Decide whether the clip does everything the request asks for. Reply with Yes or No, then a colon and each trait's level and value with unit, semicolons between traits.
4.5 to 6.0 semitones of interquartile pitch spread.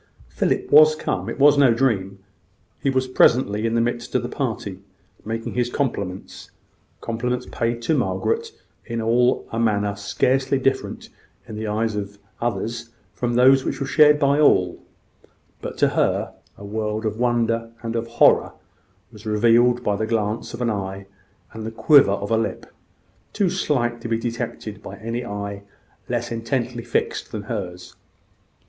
No: narrow, 2.6 semitones